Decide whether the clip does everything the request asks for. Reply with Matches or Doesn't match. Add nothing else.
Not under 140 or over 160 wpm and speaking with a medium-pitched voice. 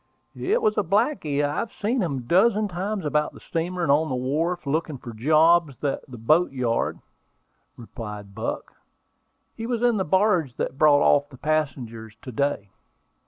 Doesn't match